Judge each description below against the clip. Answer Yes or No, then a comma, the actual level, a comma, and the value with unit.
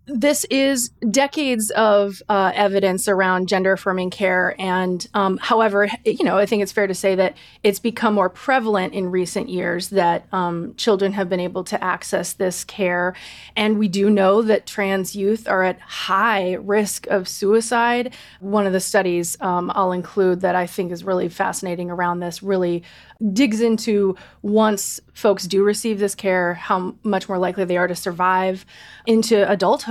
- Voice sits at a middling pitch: No, high, 195 Hz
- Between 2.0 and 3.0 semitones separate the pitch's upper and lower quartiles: Yes, narrow, 2.6 semitones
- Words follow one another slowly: No, average, 175 wpm